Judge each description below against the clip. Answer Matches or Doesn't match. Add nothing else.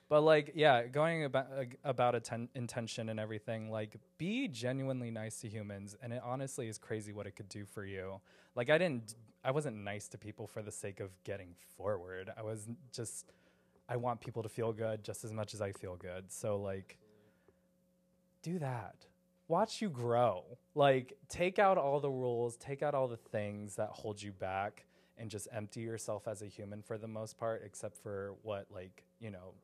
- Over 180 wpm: Matches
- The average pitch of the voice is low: Matches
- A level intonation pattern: Doesn't match